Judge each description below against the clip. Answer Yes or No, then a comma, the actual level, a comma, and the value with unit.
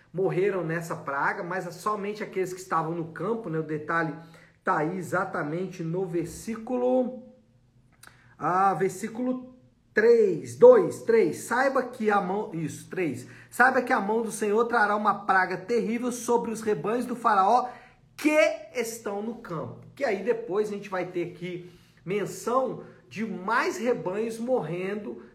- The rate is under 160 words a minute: Yes, average, 145 wpm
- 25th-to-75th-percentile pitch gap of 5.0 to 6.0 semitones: Yes, wide, 5.5 semitones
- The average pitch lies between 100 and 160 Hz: No, high, 205 Hz